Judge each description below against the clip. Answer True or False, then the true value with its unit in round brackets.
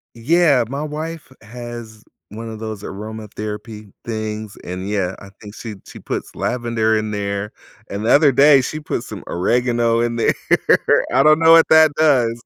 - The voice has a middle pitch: False (115 Hz)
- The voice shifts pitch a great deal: False (4.4 semitones)